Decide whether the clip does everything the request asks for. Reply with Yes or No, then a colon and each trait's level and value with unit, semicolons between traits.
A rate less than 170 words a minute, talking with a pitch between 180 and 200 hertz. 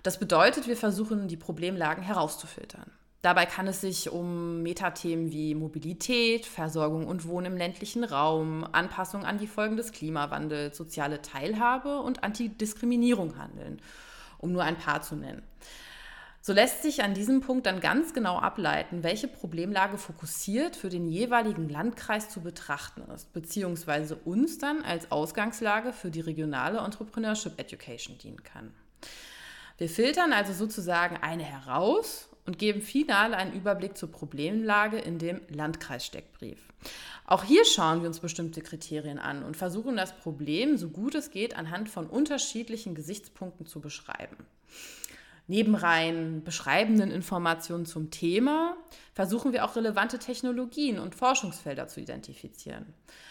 Yes: average, 140 wpm; medium, 185 Hz